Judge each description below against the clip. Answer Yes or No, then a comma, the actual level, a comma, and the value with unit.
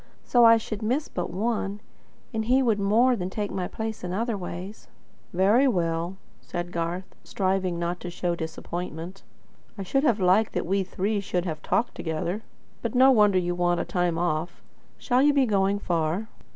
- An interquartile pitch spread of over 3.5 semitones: Yes, average, 3.9 semitones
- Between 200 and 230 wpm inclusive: No, average, 180 wpm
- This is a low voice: No, high, 190 Hz